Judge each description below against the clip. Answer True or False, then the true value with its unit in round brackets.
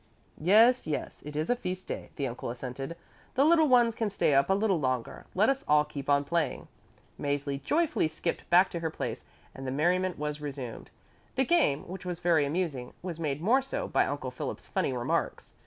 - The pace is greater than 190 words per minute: True (200 wpm)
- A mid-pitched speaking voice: True (165 Hz)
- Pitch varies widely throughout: True (6.1 semitones)